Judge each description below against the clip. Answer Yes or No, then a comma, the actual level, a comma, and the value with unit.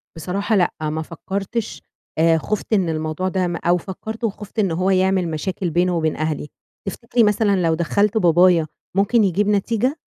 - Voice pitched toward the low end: No, medium, 185 Hz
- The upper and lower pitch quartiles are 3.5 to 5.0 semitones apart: Yes, average, 3.8 semitones